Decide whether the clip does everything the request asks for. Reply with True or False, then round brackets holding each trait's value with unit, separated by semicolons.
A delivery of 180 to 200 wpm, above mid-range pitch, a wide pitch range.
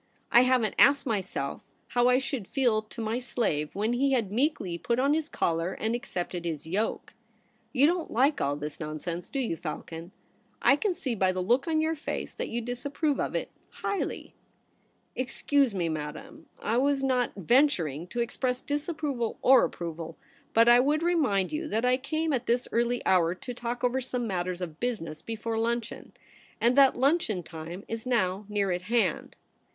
True (190 wpm; 235 Hz; 6.5 semitones)